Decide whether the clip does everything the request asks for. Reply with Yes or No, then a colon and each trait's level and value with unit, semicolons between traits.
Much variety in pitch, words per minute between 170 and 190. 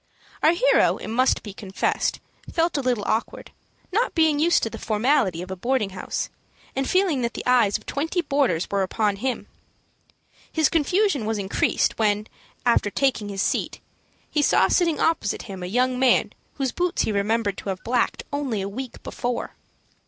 Yes: wide, 6.1 semitones; average, 175 wpm